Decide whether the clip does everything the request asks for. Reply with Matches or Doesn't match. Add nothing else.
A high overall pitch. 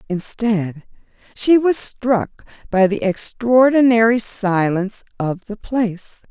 Matches